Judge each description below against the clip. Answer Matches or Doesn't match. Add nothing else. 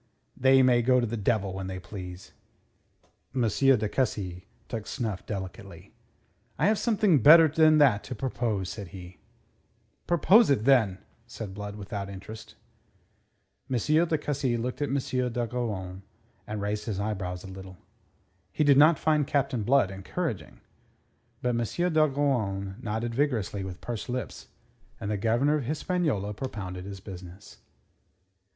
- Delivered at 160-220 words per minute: Doesn't match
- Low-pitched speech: Matches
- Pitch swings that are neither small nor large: Doesn't match